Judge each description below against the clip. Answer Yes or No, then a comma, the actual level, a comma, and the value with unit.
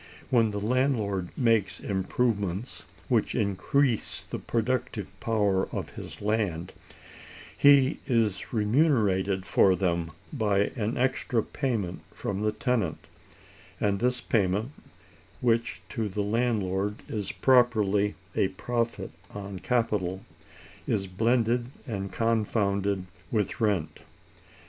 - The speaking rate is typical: No, slow, 105 wpm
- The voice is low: Yes, low, 105 Hz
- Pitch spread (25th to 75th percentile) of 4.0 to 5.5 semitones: No, average, 3.4 semitones